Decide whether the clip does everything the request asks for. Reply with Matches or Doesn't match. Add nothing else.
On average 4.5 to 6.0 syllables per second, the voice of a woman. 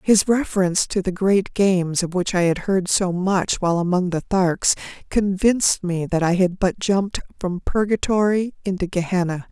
Matches